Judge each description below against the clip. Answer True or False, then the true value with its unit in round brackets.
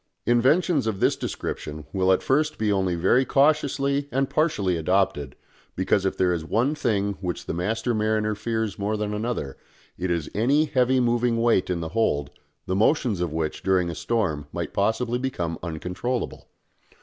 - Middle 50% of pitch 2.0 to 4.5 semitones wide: False (5.5 semitones)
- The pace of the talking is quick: False (170 wpm)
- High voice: False (105 Hz)